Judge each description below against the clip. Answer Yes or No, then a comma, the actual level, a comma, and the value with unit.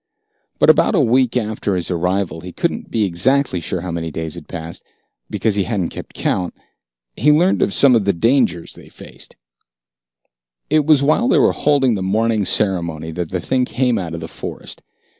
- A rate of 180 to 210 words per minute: Yes, average, 190 wpm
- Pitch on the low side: Yes, low, 100 Hz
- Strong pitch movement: Yes, wide, 6.7 semitones